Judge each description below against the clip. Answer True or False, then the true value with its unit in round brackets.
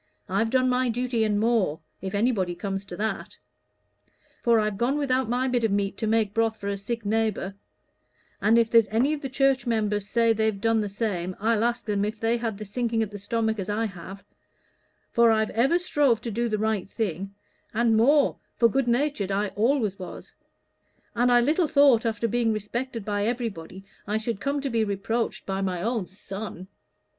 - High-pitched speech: True (225 Hz)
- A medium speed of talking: True (195 wpm)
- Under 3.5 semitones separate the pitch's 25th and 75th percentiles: True (2.9 semitones)